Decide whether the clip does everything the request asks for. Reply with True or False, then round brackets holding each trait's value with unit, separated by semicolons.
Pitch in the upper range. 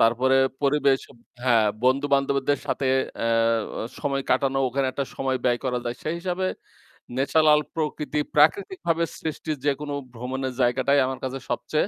False (135 Hz)